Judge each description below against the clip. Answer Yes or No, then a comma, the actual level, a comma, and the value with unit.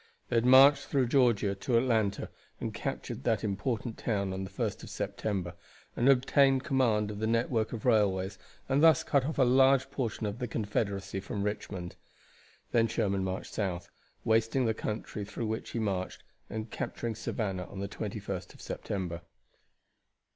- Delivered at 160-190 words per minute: Yes, average, 165 wpm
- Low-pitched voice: Yes, low, 110 Hz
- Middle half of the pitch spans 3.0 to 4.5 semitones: Yes, average, 4.0 semitones